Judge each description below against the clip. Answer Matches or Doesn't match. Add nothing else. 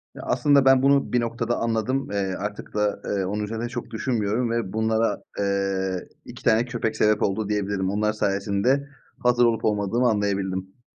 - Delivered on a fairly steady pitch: Doesn't match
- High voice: Doesn't match